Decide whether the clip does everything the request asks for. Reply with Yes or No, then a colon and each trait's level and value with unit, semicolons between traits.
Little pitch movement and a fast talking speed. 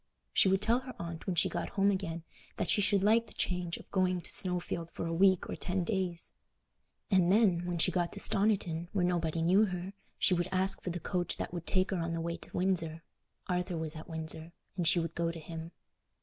Yes: narrow, 2.3 semitones; fast, 230 wpm